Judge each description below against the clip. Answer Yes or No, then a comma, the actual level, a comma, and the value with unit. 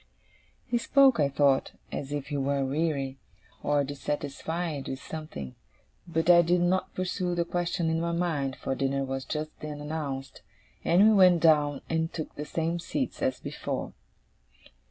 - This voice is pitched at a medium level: Yes, medium, 155 Hz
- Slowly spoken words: No, average, 160 wpm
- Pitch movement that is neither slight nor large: Yes, average, 3.6 semitones